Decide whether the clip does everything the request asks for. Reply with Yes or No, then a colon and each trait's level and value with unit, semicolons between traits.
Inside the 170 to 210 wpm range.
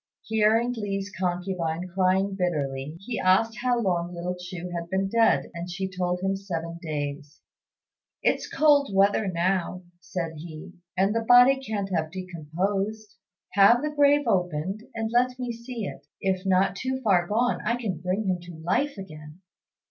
No: average, 160 wpm